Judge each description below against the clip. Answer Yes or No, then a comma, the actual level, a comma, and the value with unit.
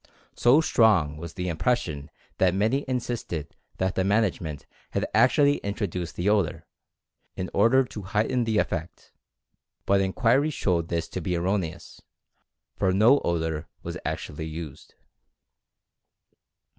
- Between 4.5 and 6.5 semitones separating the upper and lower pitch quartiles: Yes, average, 5.2 semitones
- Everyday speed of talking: No, slow, 130 wpm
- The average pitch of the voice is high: No, very low, 95 Hz